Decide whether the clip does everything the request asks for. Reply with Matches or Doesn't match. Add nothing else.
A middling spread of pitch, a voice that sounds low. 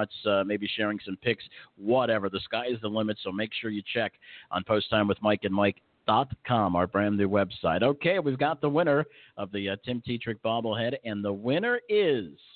Matches